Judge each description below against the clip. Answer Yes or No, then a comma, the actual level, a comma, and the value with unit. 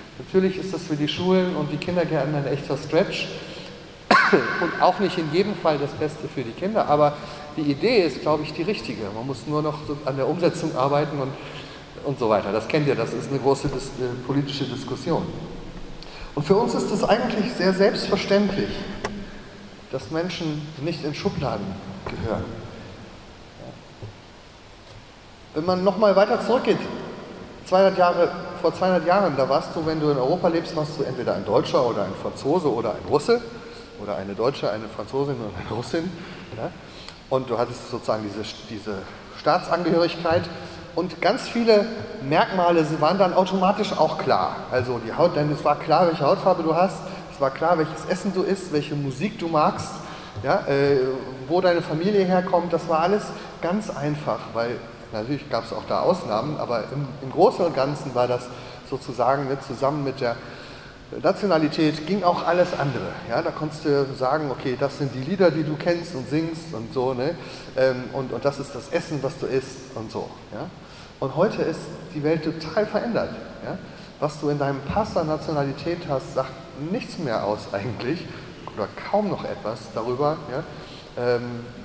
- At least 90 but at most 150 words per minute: No, average, 175 wpm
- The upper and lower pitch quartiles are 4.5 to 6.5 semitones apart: Yes, average, 4.9 semitones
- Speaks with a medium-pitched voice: Yes, medium, 150 Hz